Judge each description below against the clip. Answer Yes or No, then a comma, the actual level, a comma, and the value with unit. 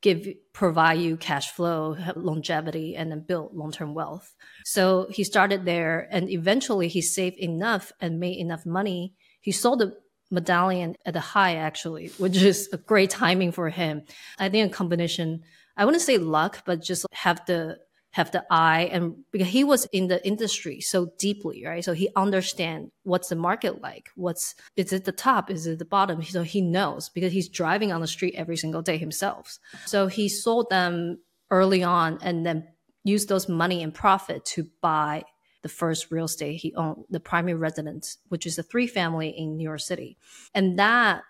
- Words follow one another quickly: No, average, 185 wpm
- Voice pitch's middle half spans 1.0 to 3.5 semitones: Yes, average, 2.8 semitones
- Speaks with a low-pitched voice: No, medium, 180 Hz